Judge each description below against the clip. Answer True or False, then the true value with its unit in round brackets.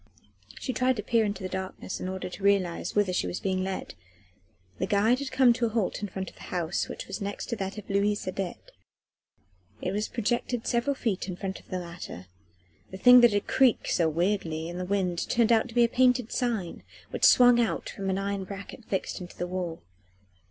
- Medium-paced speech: False (215 wpm)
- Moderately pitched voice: False (200 Hz)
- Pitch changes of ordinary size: True (4.0 semitones)